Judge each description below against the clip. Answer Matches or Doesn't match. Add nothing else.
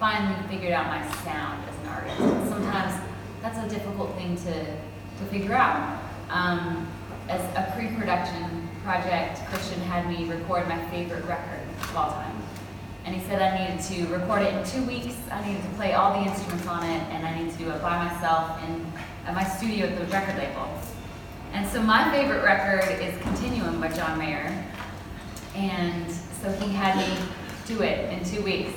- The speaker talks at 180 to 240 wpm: Matches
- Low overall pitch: Doesn't match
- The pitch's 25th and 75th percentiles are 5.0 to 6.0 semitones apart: Doesn't match